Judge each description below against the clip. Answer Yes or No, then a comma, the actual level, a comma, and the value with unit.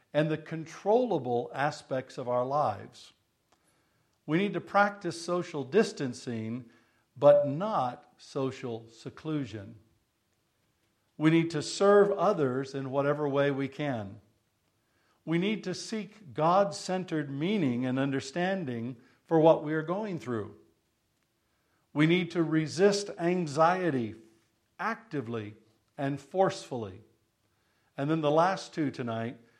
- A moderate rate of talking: No, slow, 115 wpm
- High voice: No, medium, 140 Hz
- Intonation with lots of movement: Yes, wide, 6.4 semitones